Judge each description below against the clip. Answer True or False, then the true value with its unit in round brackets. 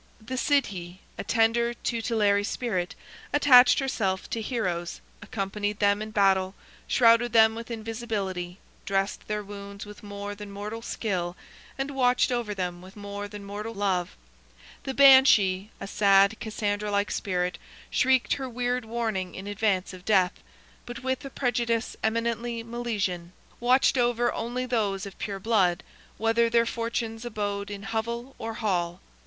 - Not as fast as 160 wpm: True (145 wpm)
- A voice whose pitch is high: True (215 Hz)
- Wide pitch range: False (3.0 semitones)